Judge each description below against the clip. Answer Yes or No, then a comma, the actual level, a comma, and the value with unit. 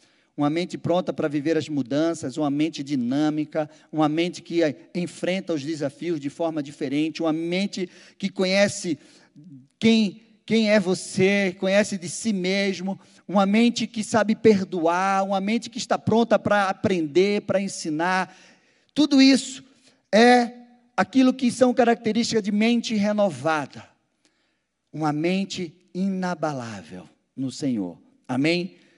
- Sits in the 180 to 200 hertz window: Yes, medium, 185 Hz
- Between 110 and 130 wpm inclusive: Yes, average, 125 wpm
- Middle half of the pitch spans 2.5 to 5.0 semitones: No, wide, 5.4 semitones